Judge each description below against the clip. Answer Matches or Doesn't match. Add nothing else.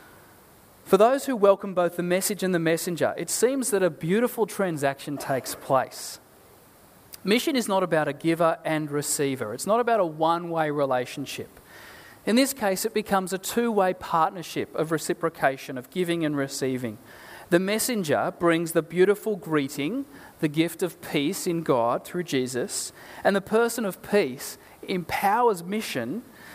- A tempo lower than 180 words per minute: Matches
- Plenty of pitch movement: Doesn't match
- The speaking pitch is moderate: Matches